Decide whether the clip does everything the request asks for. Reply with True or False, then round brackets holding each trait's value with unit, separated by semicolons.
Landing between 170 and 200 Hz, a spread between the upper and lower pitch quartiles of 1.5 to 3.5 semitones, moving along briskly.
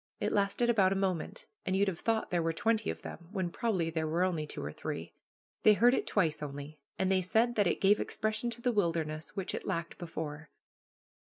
False (185 Hz; 4.6 semitones; 215 wpm)